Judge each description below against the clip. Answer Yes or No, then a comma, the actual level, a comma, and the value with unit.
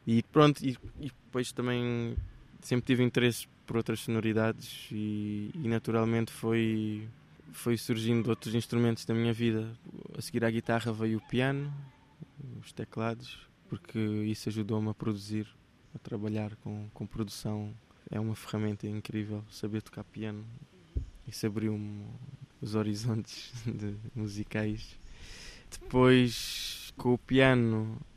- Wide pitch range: No, narrow, 2.5 semitones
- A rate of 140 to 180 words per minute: No, average, 130 wpm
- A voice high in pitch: No, low, 115 Hz